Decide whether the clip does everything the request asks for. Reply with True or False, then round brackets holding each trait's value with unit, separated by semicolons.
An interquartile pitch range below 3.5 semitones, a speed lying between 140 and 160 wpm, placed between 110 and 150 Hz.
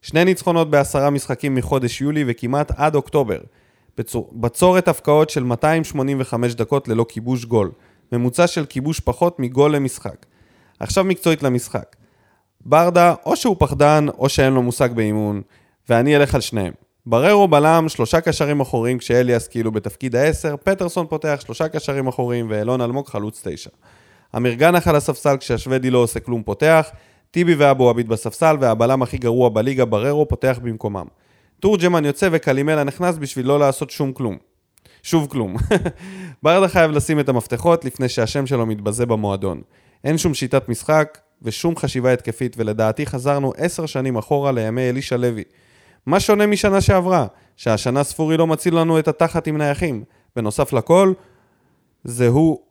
False (4.8 semitones; 150 wpm; 135 Hz)